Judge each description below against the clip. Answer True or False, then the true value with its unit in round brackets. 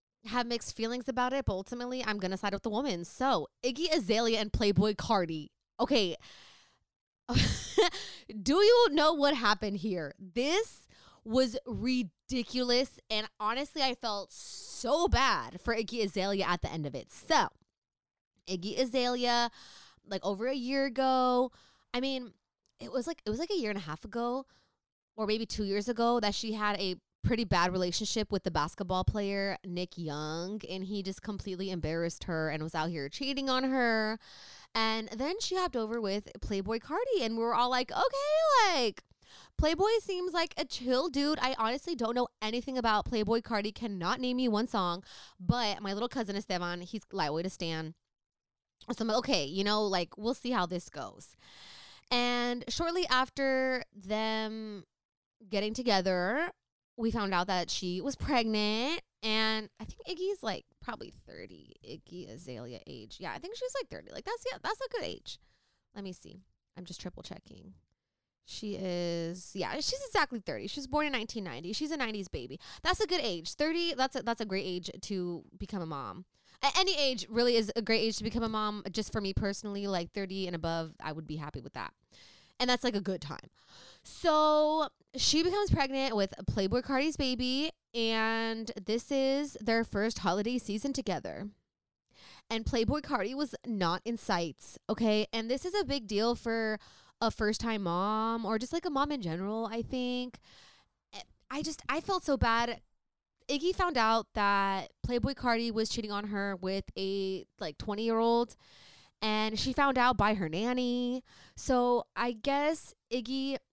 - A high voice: True (225 Hz)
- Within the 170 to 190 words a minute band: True (175 wpm)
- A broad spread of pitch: False (4.7 semitones)